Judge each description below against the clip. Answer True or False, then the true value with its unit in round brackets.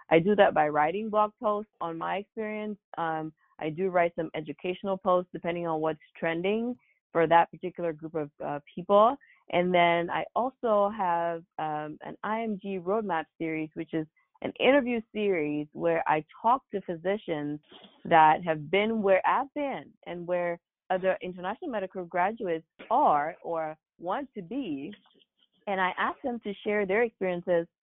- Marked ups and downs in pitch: False (4.1 semitones)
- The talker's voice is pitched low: False (180 Hz)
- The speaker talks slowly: False (155 wpm)